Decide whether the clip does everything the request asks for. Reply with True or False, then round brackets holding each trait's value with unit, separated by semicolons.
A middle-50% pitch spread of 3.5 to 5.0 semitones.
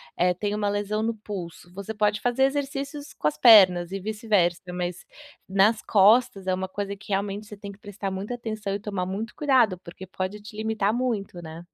False (2.6 semitones)